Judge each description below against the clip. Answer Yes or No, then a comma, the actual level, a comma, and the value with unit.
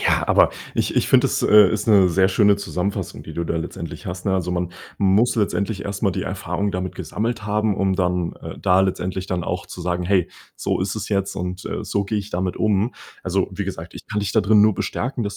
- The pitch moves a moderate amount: No, narrow, 2.2 semitones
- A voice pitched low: Yes, very low, 95 Hz